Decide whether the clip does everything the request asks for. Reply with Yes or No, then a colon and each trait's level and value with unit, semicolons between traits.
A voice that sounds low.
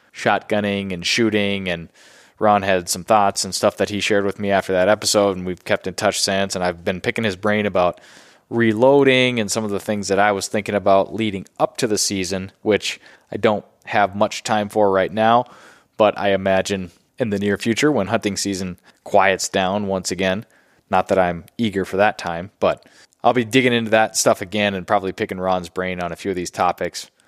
Yes: low, 100 Hz